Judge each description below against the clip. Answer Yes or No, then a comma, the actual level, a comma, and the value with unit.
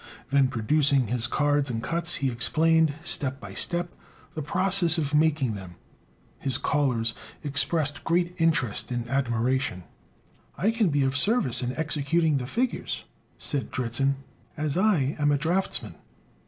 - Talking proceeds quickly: No, average, 140 wpm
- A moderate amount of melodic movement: Yes, average, 4.2 semitones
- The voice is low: No, medium, 145 Hz